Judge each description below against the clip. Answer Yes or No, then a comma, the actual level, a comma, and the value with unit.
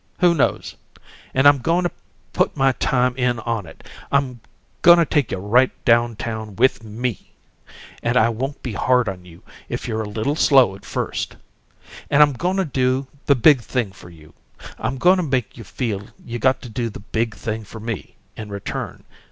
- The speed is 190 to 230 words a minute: Yes, average, 195 wpm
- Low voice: Yes, low, 120 Hz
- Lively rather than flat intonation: No, average, 3.7 semitones